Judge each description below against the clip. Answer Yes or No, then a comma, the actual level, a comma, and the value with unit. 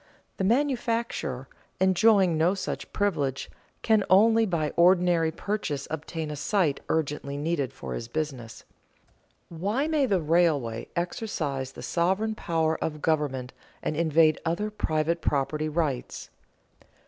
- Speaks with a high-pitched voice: No, medium, 165 Hz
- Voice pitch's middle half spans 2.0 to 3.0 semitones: No, average, 4.8 semitones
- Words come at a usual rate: No, slow, 125 wpm